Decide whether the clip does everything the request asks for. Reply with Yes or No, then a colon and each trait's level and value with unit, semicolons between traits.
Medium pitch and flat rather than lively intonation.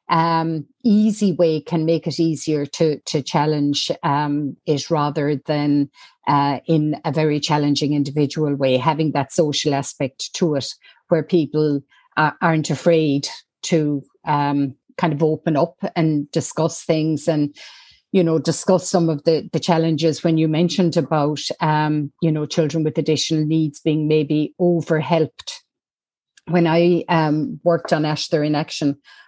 Yes: medium, 155 Hz; narrow, 2.1 semitones